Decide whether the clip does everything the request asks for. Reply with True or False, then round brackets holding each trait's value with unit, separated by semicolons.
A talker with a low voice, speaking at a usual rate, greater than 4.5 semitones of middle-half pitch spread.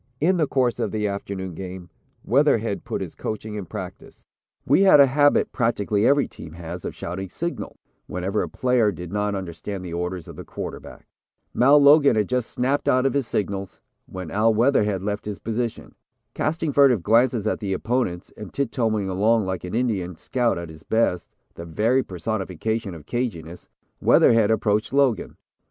True (105 Hz; 175 wpm; 5.1 semitones)